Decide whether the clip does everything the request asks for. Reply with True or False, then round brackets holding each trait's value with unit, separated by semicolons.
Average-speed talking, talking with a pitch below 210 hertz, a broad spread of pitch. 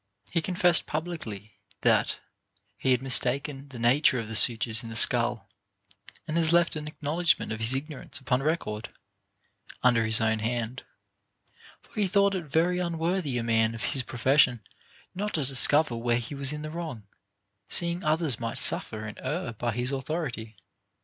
True (170 wpm; 135 Hz; 5.7 semitones)